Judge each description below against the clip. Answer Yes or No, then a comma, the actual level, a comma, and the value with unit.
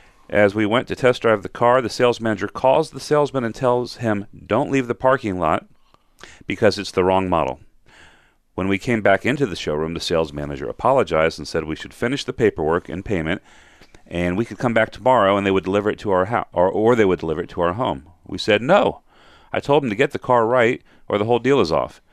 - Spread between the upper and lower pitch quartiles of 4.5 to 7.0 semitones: Yes, wide, 5.6 semitones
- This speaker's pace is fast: Yes, fast, 235 wpm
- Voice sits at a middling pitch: No, low, 105 Hz